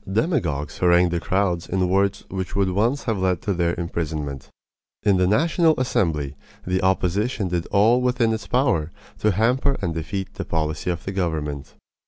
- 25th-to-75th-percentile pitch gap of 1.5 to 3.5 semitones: No, average, 4.5 semitones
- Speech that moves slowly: No, average, 170 wpm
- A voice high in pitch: No, very low, 95 Hz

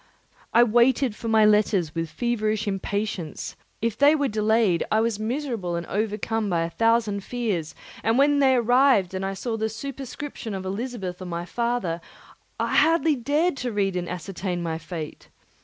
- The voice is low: No, high, 215 Hz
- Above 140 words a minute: Yes, average, 170 wpm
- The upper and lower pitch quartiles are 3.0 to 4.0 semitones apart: No, average, 4.4 semitones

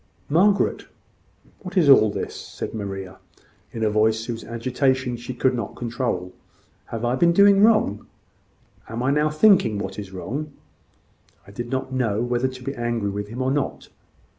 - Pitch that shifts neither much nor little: Yes, average, 4.1 semitones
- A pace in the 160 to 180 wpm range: Yes, average, 165 wpm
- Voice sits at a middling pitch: No, low, 120 Hz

